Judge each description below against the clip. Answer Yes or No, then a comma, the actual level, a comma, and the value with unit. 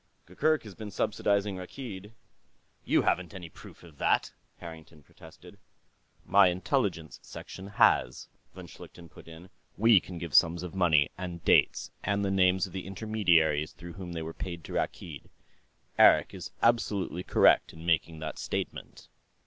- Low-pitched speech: Yes, very low, 90 Hz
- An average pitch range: Yes, average, 3.3 semitones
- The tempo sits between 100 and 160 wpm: Yes, average, 155 wpm